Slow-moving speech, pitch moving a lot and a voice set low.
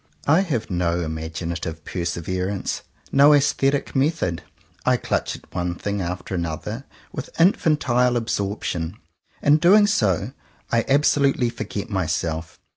Yes: slow, 120 wpm; wide, 8.3 semitones; low, 100 Hz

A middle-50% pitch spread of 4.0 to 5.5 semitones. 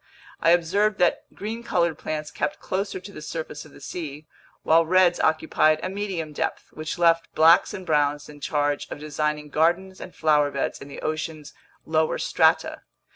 No: average, 3.0 semitones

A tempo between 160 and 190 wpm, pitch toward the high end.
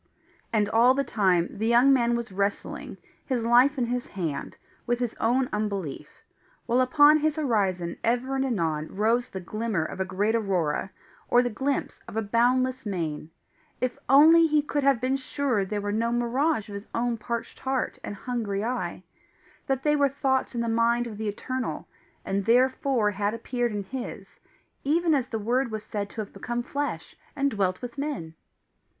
Yes: average, 180 wpm; high, 235 Hz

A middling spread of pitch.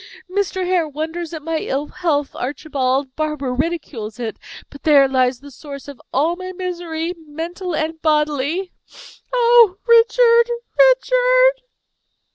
Yes: average, 4.7 semitones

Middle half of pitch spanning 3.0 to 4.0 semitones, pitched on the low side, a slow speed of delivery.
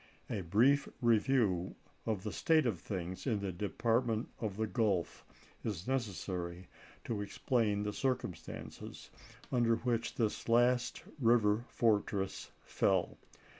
Yes: average, 3.3 semitones; low, 110 Hz; slow, 120 wpm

